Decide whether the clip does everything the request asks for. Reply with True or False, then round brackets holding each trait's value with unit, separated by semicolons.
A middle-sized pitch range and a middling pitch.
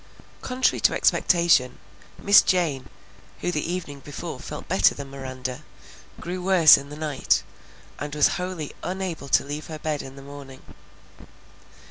True (4.3 semitones; 150 Hz)